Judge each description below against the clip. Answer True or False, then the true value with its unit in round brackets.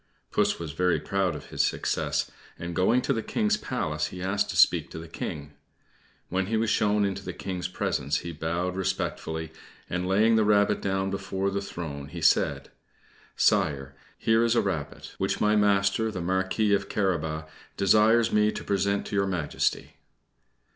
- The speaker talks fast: False (175 wpm)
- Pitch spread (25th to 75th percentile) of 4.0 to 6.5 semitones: False (3.5 semitones)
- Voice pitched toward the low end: True (95 Hz)